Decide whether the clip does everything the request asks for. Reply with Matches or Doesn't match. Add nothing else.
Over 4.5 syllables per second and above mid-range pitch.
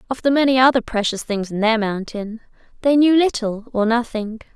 Matches